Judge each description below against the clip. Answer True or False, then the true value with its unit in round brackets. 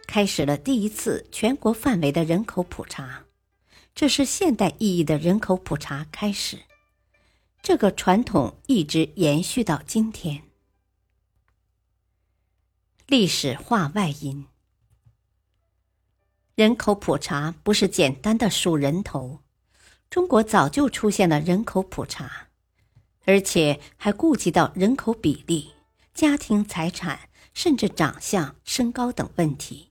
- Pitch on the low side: False (170 Hz)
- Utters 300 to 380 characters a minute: False (180 characters per minute)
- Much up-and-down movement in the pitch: True (8.0 semitones)